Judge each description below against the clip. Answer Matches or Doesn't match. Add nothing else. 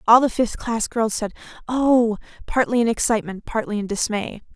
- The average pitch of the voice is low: Doesn't match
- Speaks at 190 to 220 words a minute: Doesn't match